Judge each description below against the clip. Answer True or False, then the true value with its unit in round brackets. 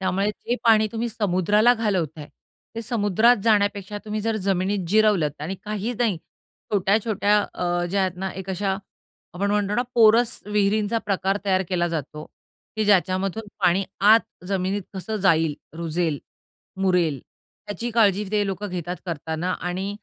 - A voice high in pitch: True (195 Hz)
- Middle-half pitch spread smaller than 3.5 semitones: True (2.8 semitones)